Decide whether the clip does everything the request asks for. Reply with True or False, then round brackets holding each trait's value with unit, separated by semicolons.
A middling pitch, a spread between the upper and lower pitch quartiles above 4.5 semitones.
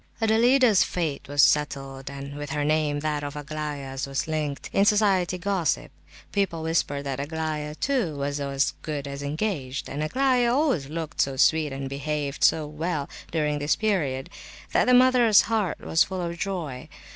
True (155 Hz; 4.9 semitones)